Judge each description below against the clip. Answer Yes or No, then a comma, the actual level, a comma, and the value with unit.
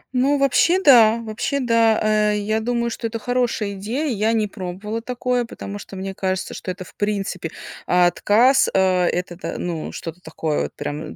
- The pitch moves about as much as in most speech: Yes, average, 4.3 semitones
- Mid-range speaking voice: No, high, 215 Hz